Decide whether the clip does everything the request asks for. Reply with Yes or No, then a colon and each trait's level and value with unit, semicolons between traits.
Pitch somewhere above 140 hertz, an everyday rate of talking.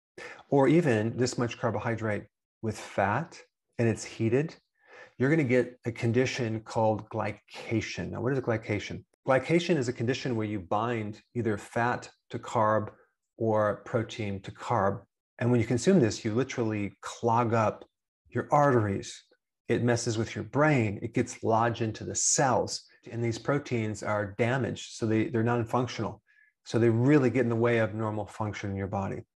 No: low, 115 Hz; average, 170 wpm